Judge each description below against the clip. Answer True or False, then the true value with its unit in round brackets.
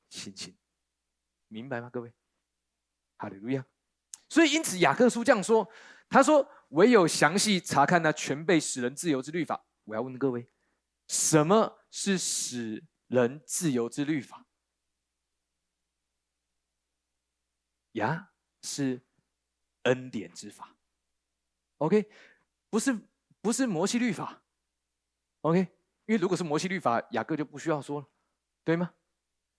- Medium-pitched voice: False (130 Hz)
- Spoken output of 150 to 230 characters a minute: True (195 characters per minute)